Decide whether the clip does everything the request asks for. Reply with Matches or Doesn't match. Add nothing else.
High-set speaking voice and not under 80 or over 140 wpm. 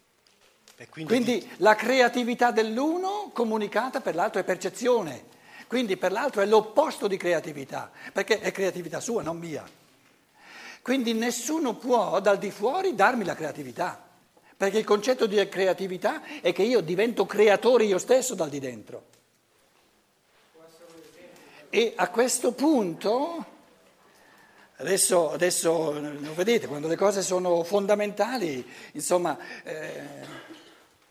Matches